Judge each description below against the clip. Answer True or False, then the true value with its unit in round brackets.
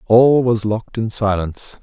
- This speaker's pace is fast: False (165 wpm)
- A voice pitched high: False (110 Hz)